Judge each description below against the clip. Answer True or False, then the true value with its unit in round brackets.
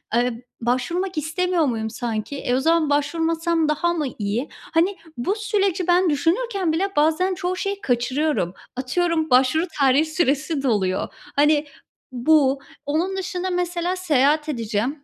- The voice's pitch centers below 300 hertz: False (310 Hz)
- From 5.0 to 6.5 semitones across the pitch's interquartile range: True (5.3 semitones)